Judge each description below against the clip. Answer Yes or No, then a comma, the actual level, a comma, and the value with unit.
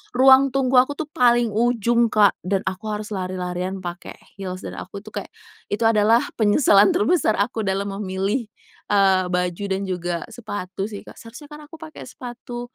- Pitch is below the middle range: No, high, 210 Hz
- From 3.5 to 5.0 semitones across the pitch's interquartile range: Yes, average, 4.1 semitones